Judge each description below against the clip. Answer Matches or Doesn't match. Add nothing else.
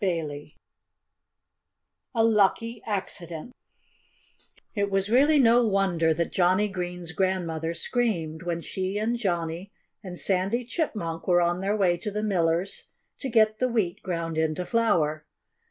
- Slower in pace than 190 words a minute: Matches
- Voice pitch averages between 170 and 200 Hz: Matches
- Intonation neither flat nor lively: Matches